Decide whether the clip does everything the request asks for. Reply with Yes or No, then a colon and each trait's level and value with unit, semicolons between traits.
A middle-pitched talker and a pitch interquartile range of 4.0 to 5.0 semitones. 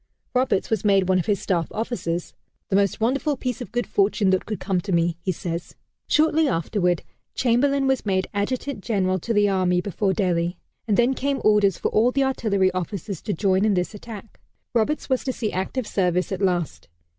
No: high, 200 Hz; average, 4.5 semitones